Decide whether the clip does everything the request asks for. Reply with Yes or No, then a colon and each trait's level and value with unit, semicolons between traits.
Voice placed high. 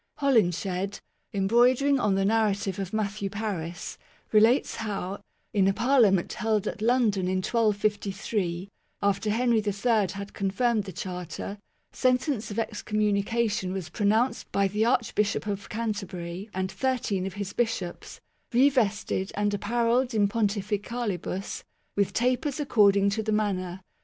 Yes: high, 205 Hz